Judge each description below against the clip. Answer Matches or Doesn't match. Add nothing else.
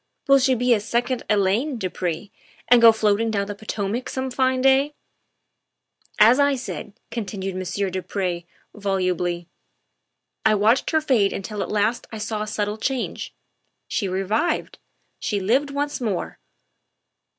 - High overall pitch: Matches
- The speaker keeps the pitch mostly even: Doesn't match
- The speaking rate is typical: Matches